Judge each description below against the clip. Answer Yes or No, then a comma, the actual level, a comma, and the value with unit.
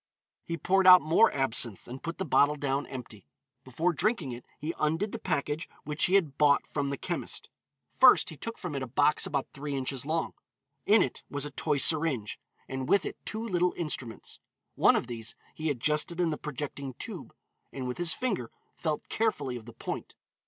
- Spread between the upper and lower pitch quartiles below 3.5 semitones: No, average, 4.3 semitones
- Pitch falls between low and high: Yes, medium, 150 Hz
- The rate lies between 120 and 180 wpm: No, average, 195 wpm